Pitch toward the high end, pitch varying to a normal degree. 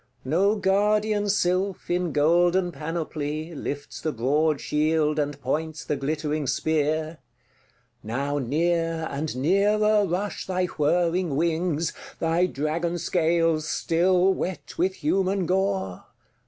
No: medium, 165 Hz; average, 3.3 semitones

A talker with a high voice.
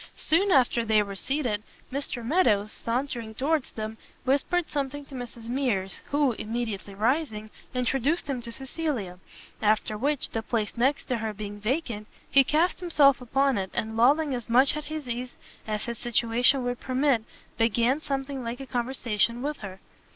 Yes: high, 245 Hz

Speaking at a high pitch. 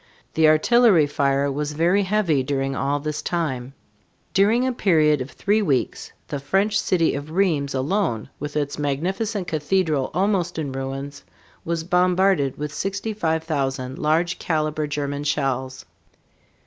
No: medium, 155 Hz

